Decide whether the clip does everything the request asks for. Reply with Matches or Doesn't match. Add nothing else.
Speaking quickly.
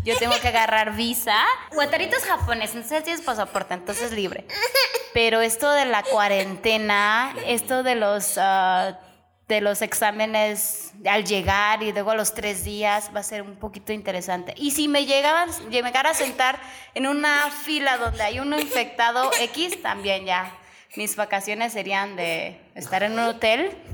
Doesn't match